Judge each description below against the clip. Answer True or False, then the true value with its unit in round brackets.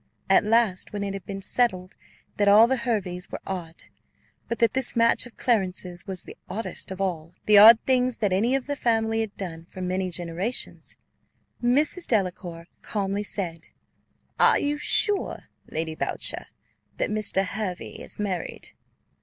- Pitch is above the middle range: True (200 Hz)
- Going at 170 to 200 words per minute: False (160 wpm)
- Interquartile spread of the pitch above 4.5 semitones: False (4.1 semitones)